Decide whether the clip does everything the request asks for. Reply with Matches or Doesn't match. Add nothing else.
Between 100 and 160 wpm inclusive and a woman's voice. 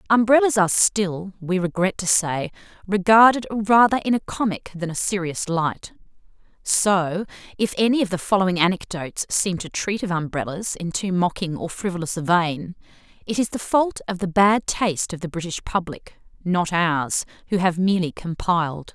Doesn't match